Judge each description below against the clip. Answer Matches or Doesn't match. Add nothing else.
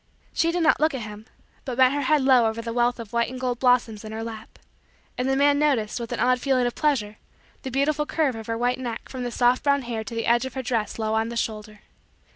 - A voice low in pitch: Doesn't match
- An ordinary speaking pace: Doesn't match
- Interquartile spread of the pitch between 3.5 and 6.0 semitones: Doesn't match